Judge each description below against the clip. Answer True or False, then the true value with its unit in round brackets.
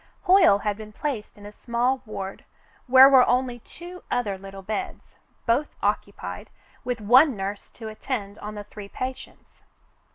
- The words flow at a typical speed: True (155 wpm)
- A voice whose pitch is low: False (230 Hz)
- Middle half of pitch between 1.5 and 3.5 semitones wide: False (4.1 semitones)